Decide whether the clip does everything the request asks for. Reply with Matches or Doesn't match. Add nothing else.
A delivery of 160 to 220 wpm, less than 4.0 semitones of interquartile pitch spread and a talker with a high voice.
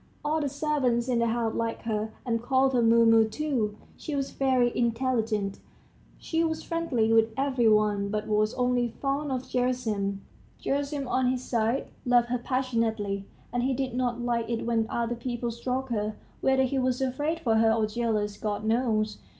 Matches